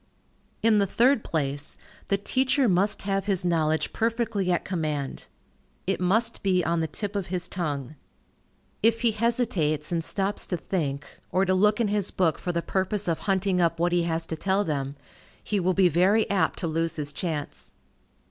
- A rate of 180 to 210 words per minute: Yes, average, 185 wpm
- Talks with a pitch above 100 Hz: Yes, medium, 185 Hz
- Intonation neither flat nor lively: Yes, average, 3.9 semitones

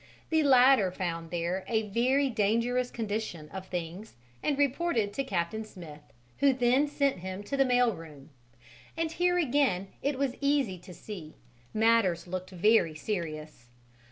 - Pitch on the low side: No, high, 215 Hz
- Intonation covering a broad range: Yes, wide, 6.9 semitones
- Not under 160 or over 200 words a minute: No, average, 150 wpm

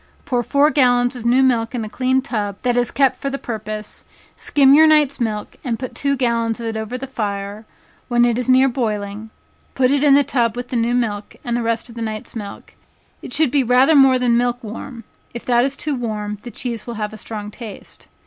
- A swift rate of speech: Yes, fast, 230 wpm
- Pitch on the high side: Yes, high, 240 Hz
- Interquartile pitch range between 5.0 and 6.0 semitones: No, average, 2.9 semitones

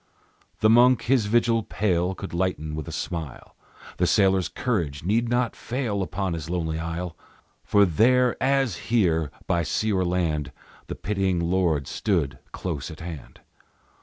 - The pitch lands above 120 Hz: No, very low, 95 Hz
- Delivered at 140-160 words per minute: Yes, average, 150 wpm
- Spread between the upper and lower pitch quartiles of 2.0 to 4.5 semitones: No, average, 5.1 semitones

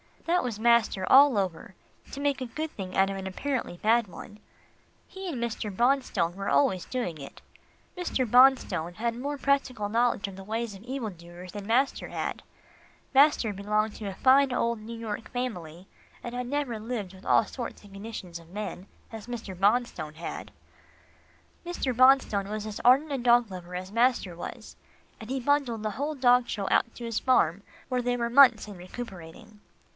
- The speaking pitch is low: No, high, 225 Hz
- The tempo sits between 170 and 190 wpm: Yes, average, 180 wpm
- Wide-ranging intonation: No, average, 4.5 semitones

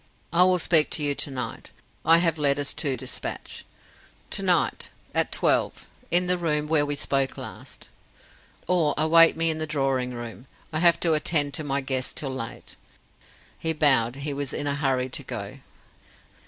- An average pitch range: Yes, average, 3.1 semitones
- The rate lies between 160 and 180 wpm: Yes, average, 175 wpm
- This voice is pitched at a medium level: Yes, medium, 145 Hz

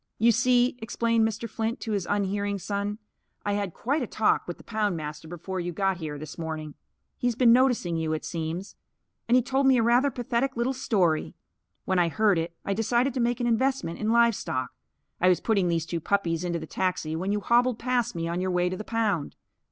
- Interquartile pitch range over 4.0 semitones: Yes, wide, 5.5 semitones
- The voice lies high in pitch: Yes, high, 205 Hz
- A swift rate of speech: Yes, fast, 215 wpm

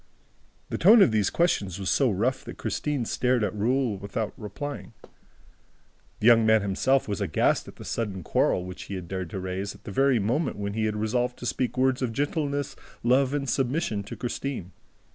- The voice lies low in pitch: Yes, low, 115 Hz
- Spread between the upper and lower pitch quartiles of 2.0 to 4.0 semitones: No, average, 4.8 semitones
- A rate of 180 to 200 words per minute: Yes, average, 195 wpm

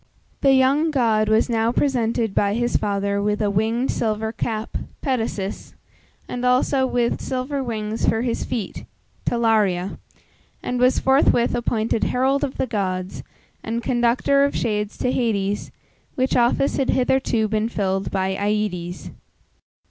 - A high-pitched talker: Yes, high, 230 Hz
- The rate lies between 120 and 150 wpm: Yes, average, 140 wpm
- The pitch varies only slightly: No, average, 3.3 semitones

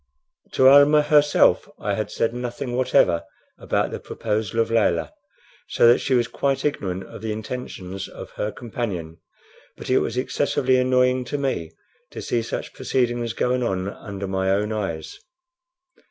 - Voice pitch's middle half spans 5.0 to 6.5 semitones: No, average, 4.5 semitones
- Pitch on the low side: Yes, low, 120 Hz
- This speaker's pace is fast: No, average, 155 wpm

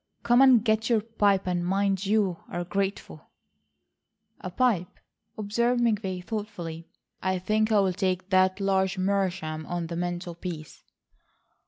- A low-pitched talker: No, high, 190 Hz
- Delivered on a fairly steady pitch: No, average, 3.2 semitones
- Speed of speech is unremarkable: No, slow, 130 wpm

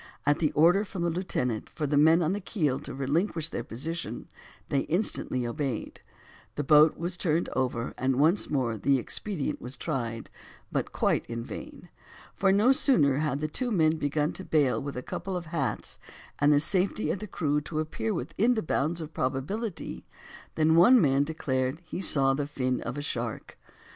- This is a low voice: No, medium, 150 Hz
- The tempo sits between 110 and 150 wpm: No, average, 185 wpm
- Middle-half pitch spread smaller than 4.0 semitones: No, average, 4.3 semitones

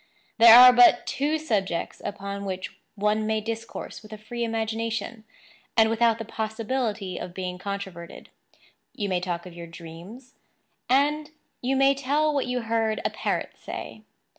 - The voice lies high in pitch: Yes, high, 220 Hz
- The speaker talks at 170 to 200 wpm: No, average, 155 wpm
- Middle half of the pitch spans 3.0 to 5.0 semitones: Yes, average, 3.7 semitones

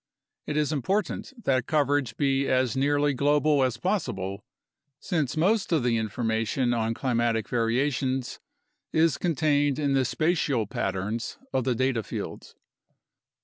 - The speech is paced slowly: Yes, slow, 130 wpm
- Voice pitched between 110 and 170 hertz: Yes, low, 135 Hz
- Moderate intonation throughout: Yes, average, 4.1 semitones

